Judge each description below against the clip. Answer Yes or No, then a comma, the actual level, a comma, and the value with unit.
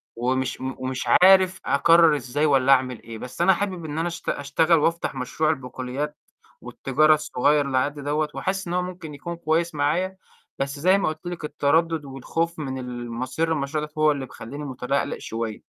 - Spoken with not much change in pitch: No, average, 4.0 semitones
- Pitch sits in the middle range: Yes, medium, 150 Hz